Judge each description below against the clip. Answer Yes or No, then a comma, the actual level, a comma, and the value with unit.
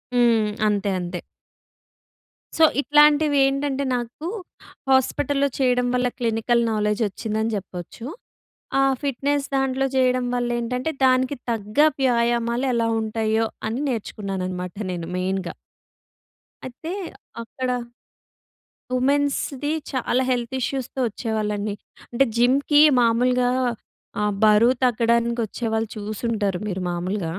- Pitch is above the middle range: Yes, high, 235 Hz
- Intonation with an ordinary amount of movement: Yes, average, 3.6 semitones